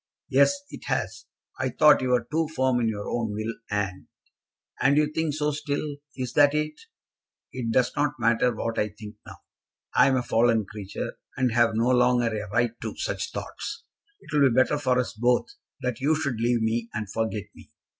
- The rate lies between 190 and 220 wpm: Yes, average, 200 wpm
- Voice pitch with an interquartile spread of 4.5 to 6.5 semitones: No, average, 4.0 semitones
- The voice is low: Yes, low, 120 Hz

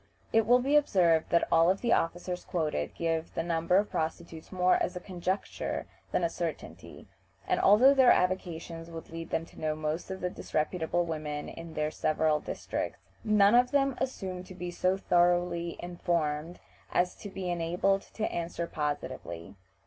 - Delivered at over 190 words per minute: No, average, 165 wpm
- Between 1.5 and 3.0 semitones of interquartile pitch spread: Yes, narrow, 2.5 semitones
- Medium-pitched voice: Yes, medium, 175 Hz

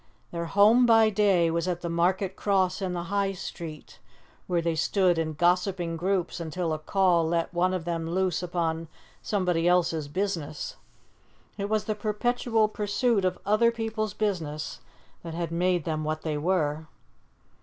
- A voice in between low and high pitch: Yes, medium, 180 Hz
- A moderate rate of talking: Yes, average, 160 wpm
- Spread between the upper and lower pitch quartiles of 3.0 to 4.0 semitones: Yes, average, 3.3 semitones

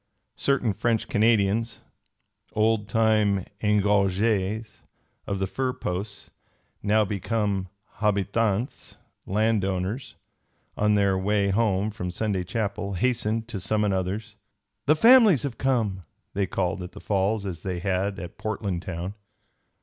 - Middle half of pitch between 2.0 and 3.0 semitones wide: Yes, narrow, 2.5 semitones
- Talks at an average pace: No, slow, 120 wpm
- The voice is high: No, low, 105 Hz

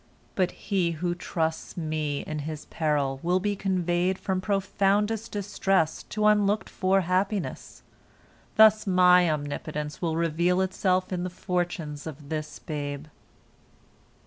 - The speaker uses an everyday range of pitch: Yes, average, 3.7 semitones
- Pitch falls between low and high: Yes, medium, 180 Hz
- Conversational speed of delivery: No, slow, 125 wpm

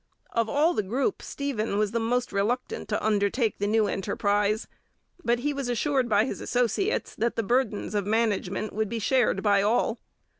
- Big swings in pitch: No, average, 3.1 semitones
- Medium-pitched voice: No, high, 225 Hz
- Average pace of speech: Yes, average, 175 wpm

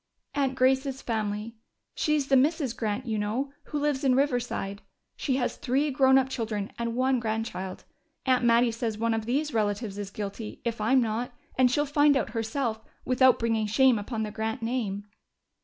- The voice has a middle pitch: No, high, 235 Hz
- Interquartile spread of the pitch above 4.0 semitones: No, average, 3.3 semitones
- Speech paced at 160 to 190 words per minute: Yes, average, 175 wpm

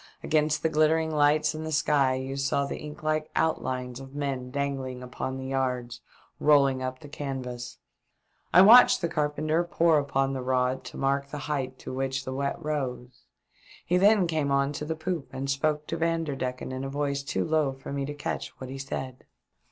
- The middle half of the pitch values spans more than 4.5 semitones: No, average, 2.8 semitones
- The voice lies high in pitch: No, medium, 140 Hz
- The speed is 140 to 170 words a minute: No, average, 190 wpm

